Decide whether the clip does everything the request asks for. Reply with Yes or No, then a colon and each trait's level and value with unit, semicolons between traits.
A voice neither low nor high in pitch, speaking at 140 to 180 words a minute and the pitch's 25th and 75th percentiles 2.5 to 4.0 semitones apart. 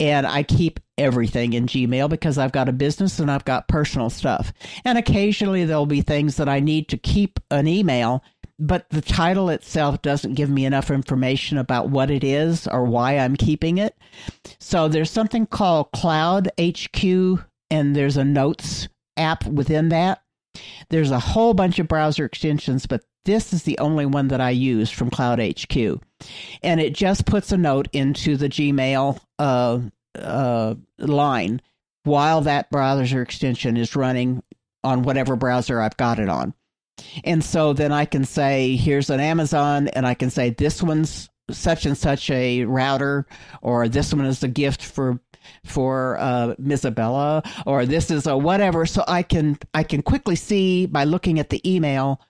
Yes: medium, 145 Hz; average, 170 wpm; average, 3.4 semitones